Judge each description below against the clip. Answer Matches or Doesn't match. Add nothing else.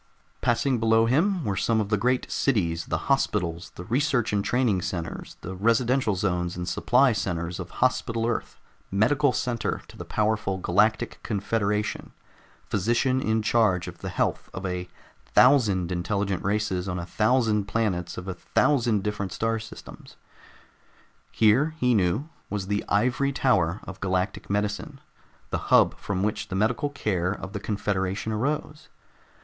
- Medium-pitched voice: Doesn't match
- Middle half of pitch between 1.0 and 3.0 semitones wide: Doesn't match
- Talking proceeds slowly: Doesn't match